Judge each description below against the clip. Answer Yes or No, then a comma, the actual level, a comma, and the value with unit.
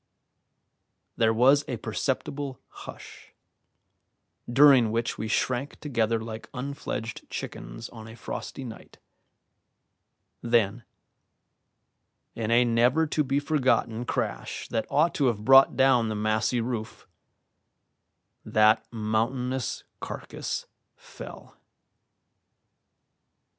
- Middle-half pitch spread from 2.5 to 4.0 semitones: Yes, average, 3.2 semitones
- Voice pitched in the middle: No, low, 120 Hz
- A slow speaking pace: Yes, slow, 95 wpm